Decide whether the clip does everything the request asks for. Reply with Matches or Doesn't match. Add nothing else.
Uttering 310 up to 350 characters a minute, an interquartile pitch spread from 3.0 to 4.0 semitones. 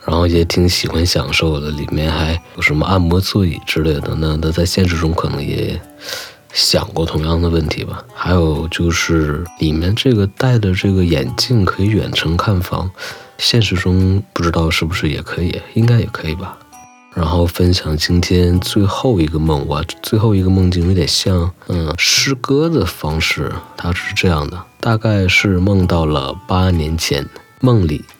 Doesn't match